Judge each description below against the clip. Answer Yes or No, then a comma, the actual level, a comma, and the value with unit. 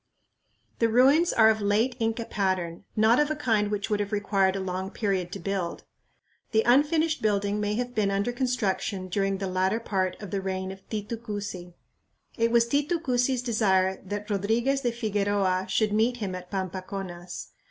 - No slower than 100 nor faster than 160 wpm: No, average, 175 wpm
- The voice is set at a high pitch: Yes, high, 205 Hz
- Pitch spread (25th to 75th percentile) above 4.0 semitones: No, average, 3.6 semitones